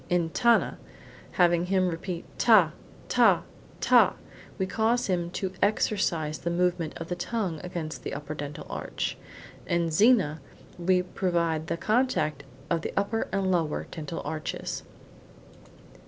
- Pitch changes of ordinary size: Yes, average, 3.0 semitones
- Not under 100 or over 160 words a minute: Yes, slow, 135 wpm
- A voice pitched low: No, medium, 175 Hz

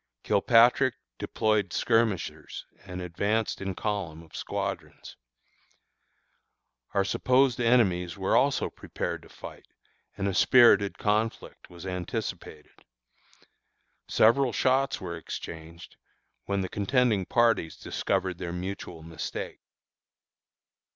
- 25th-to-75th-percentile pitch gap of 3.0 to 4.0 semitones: No, average, 4.5 semitones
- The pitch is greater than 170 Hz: No, low, 100 Hz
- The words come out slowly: Yes, slow, 100 wpm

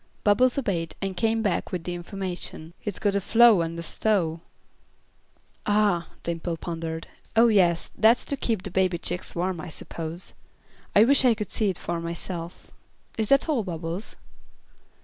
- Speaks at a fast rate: No, average, 160 wpm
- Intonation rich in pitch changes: No, average, 4.3 semitones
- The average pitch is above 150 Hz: Yes, medium, 185 Hz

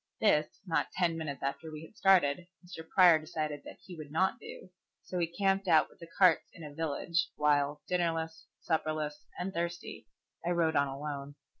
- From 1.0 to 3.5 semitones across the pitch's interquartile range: Yes, average, 2.8 semitones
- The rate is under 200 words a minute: Yes, average, 180 wpm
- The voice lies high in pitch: No, medium, 160 Hz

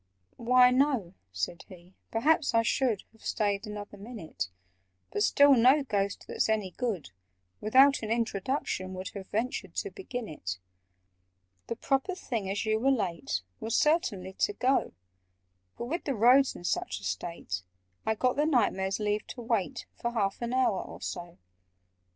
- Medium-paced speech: Yes, average, 165 wpm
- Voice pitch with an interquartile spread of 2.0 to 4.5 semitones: No, average, 5.0 semitones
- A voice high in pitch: Yes, high, 220 Hz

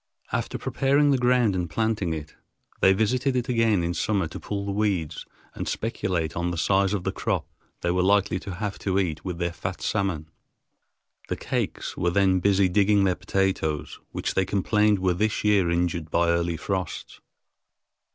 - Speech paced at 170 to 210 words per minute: Yes, average, 180 wpm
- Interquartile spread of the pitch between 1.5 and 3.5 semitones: Yes, average, 3.2 semitones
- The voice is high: No, very low, 95 Hz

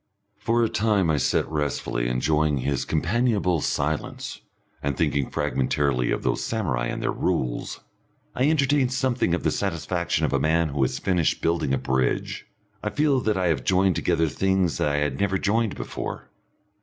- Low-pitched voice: Yes, very low, 85 Hz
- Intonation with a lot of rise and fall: Yes, wide, 6.5 semitones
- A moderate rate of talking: Yes, average, 170 wpm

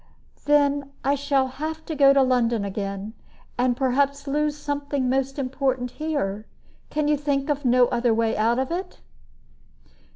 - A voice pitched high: Yes, very high, 275 Hz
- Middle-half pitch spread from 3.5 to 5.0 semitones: No, average, 2.7 semitones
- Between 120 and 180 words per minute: Yes, average, 155 wpm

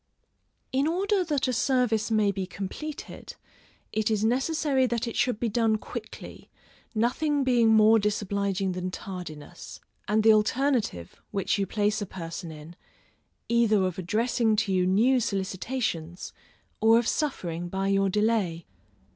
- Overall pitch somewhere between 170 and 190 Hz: No, high, 215 Hz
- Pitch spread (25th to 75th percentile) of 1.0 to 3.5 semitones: No, average, 4.2 semitones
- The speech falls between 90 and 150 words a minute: Yes, average, 140 wpm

